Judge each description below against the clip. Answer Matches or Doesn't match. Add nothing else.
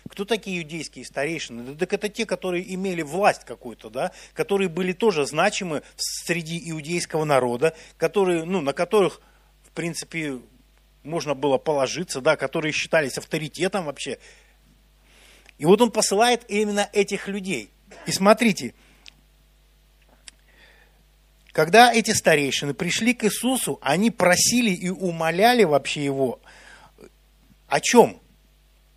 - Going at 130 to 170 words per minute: Doesn't match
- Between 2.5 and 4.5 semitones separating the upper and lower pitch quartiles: Doesn't match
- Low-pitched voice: Doesn't match